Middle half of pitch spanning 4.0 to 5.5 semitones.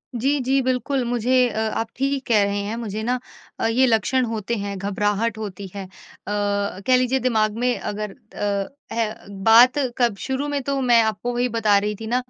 No: average, 3.5 semitones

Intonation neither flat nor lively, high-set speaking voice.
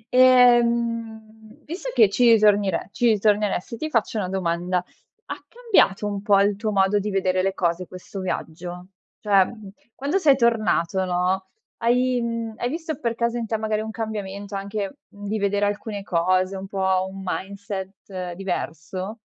Yes: average, 3.4 semitones; high, 205 Hz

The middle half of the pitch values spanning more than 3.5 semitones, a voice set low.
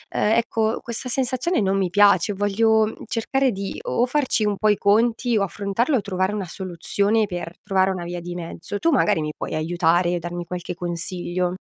No: average, 4.1 semitones; high, 200 Hz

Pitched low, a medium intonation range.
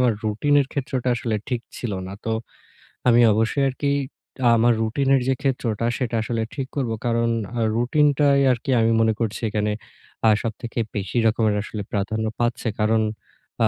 Yes: low, 115 Hz; average, 3.1 semitones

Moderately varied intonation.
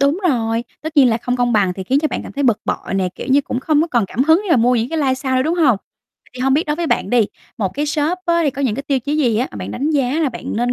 Yes: average, 4.1 semitones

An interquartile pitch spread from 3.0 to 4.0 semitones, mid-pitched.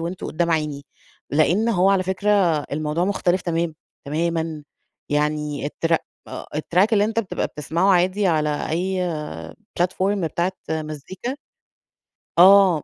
Yes: average, 3.5 semitones; medium, 170 Hz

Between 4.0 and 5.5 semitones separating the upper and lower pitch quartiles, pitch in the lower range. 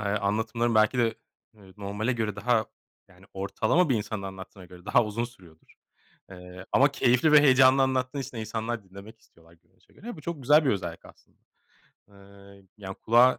Yes: average, 4.4 semitones; low, 110 Hz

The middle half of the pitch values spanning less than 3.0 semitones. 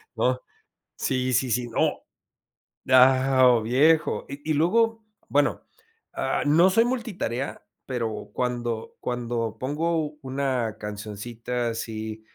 No: average, 4.4 semitones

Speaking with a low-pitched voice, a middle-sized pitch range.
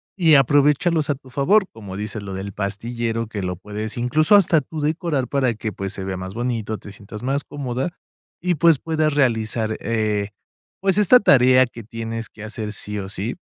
No: low, 120 Hz; wide, 5.7 semitones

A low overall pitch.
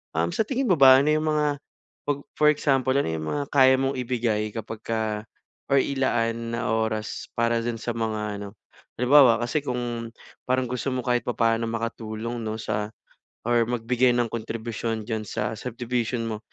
Yes: low, 115 Hz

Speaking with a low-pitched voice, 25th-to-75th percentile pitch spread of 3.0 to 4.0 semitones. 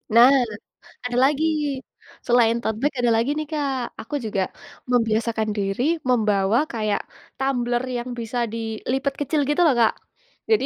No: high, 240 Hz; average, 3.3 semitones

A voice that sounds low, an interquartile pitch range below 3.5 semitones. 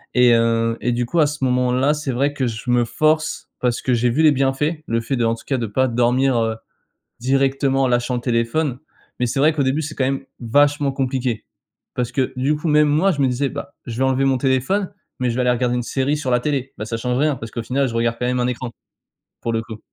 Yes: low, 130 Hz; average, 2.7 semitones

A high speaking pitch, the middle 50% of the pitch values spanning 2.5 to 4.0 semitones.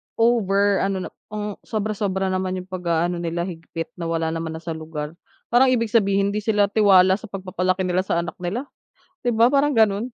Yes: high, 195 Hz; average, 3.5 semitones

